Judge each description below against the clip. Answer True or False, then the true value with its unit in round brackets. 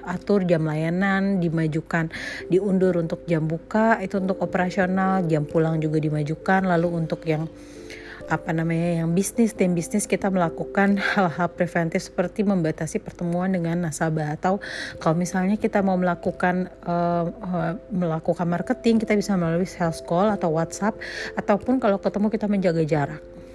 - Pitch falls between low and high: True (175 Hz)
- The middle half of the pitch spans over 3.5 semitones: False (2.8 semitones)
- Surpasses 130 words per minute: True (140 wpm)